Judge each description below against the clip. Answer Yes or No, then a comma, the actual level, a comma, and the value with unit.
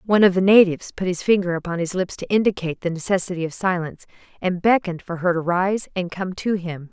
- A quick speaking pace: Yes, fast, 225 wpm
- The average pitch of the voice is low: No, medium, 180 Hz